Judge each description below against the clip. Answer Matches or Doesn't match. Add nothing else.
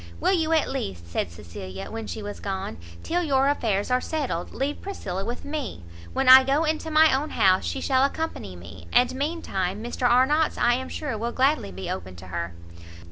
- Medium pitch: Doesn't match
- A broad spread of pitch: Matches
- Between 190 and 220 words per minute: Matches